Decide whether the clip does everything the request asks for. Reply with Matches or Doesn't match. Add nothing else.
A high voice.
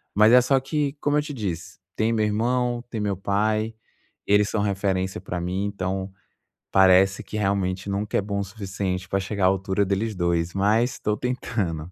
Doesn't match